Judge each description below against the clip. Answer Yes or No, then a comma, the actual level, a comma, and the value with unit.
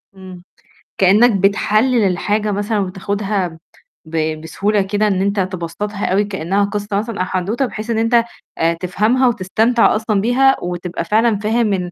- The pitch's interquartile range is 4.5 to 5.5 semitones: No, average, 2.8 semitones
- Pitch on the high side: Yes, high, 205 Hz